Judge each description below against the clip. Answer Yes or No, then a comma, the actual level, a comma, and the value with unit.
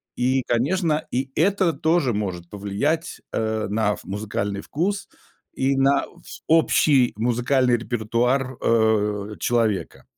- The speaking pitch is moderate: No, low, 120 Hz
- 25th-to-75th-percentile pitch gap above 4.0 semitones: Yes, average, 4.8 semitones